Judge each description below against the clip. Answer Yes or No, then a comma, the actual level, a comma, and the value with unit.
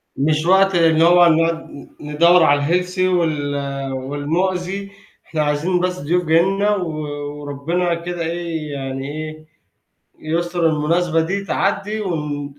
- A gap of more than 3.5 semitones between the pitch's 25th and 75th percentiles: No, average, 3.0 semitones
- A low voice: No, medium, 165 Hz